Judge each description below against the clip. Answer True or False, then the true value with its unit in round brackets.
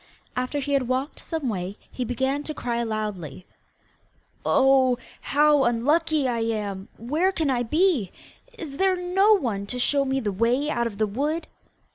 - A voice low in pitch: False (260 Hz)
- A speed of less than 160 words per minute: False (165 wpm)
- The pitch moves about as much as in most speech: True (4.7 semitones)